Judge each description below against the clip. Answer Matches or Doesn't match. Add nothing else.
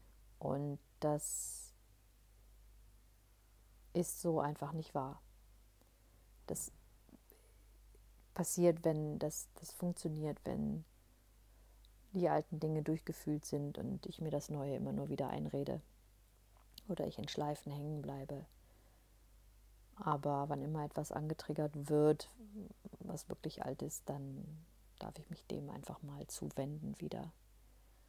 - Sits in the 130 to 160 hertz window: Matches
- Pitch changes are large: Matches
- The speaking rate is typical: Doesn't match